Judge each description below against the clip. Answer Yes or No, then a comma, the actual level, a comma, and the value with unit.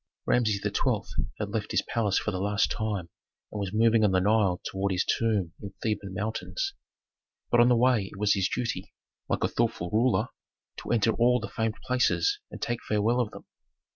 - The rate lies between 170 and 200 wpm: Yes, average, 195 wpm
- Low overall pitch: Yes, low, 110 Hz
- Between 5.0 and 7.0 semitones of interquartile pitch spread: No, average, 3.0 semitones